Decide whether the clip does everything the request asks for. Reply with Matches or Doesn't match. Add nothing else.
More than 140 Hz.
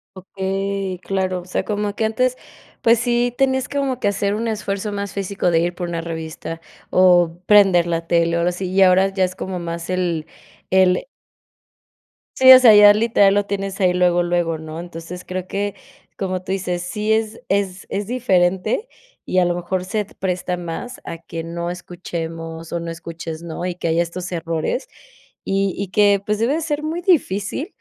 Matches